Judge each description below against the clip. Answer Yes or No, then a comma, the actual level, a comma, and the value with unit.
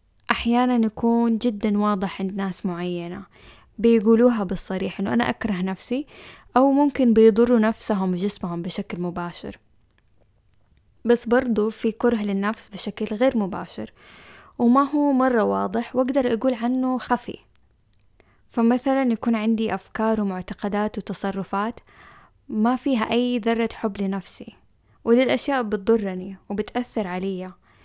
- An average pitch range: Yes, average, 3.8 semitones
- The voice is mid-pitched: No, high, 220 Hz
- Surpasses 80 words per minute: Yes, average, 110 wpm